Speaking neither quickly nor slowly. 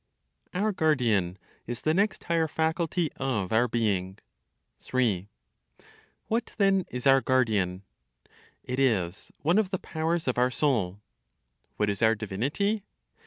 No: slow, 130 wpm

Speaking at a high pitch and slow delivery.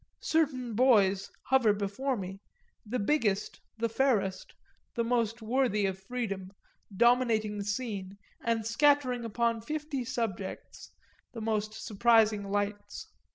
Yes: high, 225 Hz; slow, 115 wpm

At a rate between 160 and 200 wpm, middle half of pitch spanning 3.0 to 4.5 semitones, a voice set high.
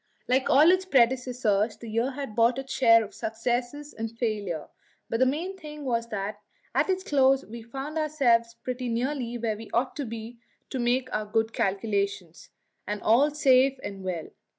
Yes: average, 175 wpm; average, 3.4 semitones; high, 240 Hz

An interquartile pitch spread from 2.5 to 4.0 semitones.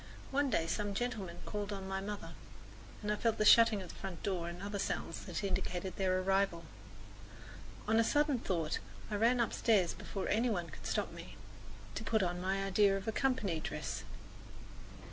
Yes: average, 3.1 semitones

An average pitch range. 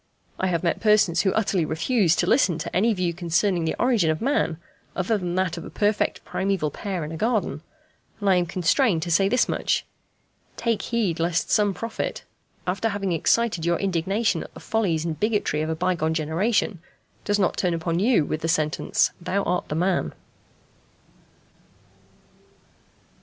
Yes: average, 4.0 semitones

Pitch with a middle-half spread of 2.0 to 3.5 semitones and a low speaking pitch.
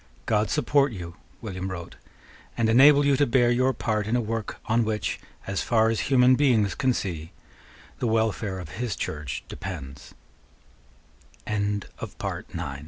No: average, 4.7 semitones; low, 110 Hz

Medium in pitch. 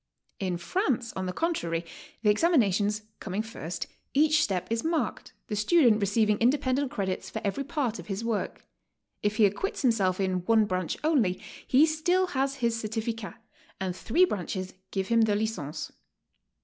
No: high, 220 Hz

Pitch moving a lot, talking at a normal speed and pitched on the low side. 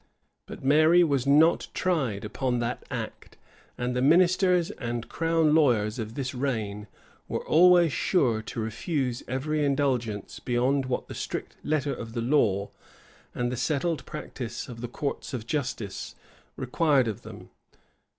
No: average, 4.5 semitones; average, 145 wpm; low, 130 Hz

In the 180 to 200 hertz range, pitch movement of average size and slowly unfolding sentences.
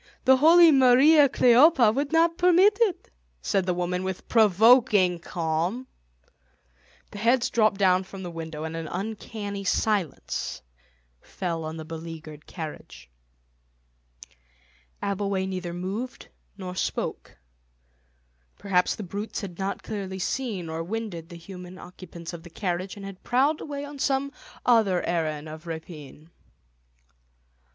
No: high, 190 Hz; wide, 5.8 semitones; slow, 130 wpm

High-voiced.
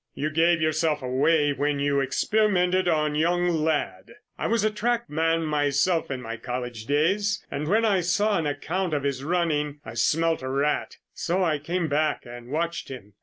No: medium, 155 Hz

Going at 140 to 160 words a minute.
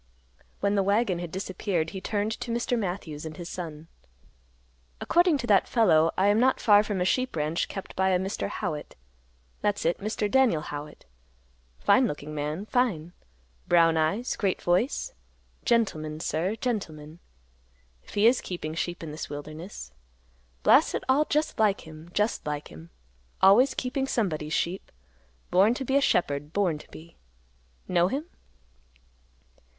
Yes: average, 155 wpm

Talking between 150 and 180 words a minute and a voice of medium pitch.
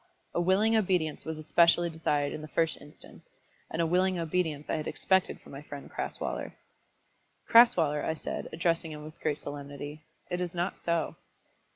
Yes: average, 170 wpm; medium, 160 Hz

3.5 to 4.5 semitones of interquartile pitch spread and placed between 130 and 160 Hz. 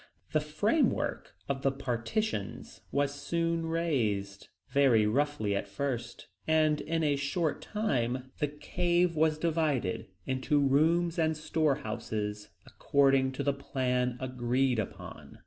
Yes: average, 4.1 semitones; medium, 140 Hz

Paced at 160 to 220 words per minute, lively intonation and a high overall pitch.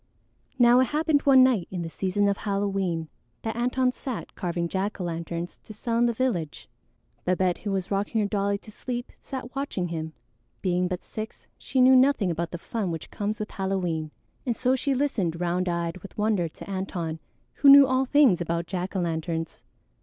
Yes: average, 190 wpm; wide, 5.9 semitones; high, 195 Hz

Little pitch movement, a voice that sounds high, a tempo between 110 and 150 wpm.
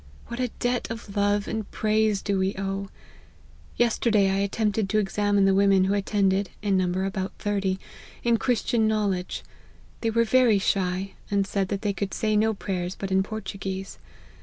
No: narrow, 2.0 semitones; high, 200 Hz; average, 170 wpm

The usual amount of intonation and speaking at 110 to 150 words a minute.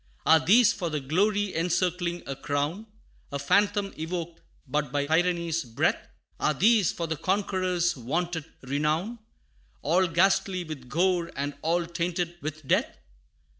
Yes: average, 3.3 semitones; slow, 135 wpm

